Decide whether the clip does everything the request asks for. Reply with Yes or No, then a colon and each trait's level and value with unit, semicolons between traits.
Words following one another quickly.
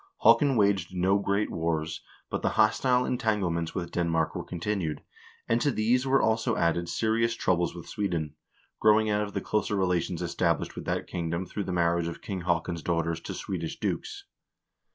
No: average, 180 wpm